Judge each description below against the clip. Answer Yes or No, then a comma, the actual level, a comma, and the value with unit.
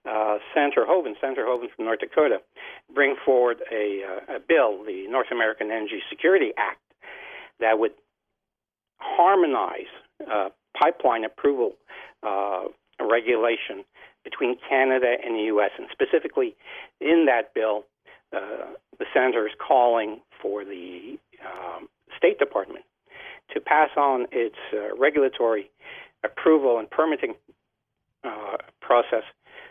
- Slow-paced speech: Yes, slow, 120 wpm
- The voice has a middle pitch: Yes, medium, 145 Hz